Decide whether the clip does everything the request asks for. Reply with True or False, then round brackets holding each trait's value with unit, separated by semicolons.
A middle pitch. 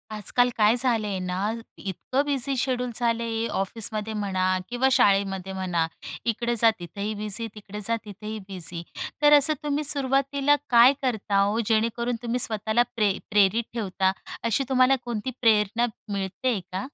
False (225 Hz)